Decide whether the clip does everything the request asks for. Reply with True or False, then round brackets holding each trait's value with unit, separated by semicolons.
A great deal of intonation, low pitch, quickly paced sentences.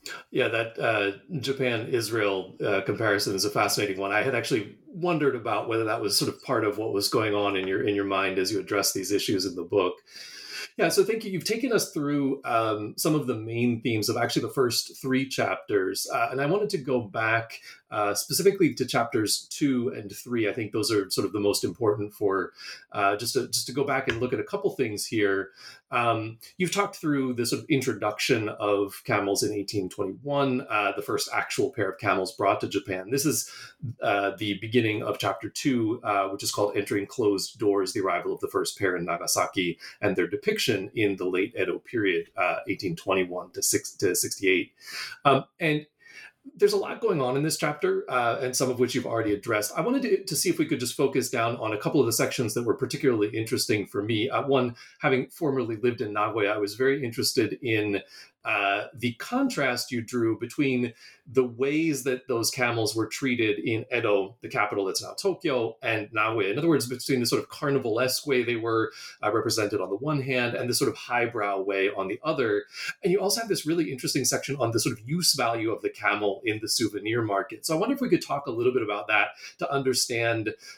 True (8.4 semitones; 130 Hz; 220 wpm)